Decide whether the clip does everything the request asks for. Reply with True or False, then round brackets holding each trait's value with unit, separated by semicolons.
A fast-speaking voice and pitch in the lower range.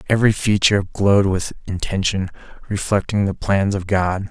False (140 wpm; 100 Hz)